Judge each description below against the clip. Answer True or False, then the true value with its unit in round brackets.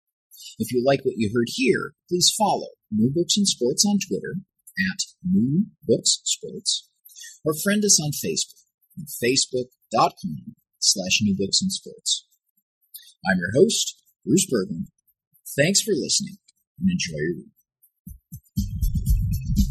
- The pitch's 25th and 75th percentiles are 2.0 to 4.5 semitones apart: False (5.6 semitones)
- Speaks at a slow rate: True (130 wpm)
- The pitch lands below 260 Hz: True (190 Hz)